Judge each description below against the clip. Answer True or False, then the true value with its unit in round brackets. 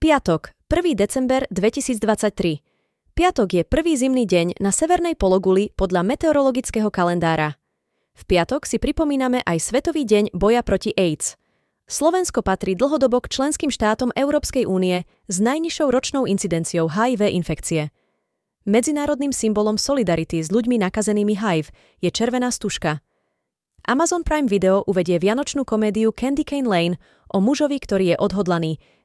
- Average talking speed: True (130 wpm)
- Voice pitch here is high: True (215 Hz)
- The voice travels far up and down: True (6.5 semitones)